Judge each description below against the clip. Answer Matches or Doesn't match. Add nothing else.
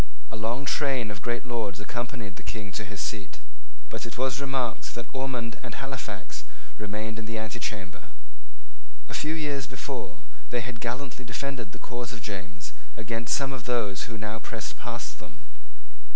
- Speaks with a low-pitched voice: Matches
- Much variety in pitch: Doesn't match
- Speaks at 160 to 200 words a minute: Matches